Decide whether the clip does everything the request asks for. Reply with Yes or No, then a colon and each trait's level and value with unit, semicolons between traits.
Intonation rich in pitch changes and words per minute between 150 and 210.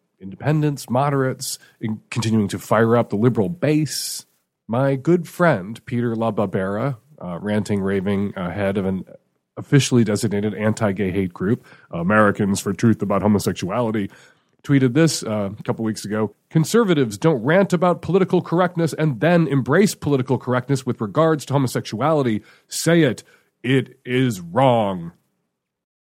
No: wide, 6.0 semitones; slow, 135 wpm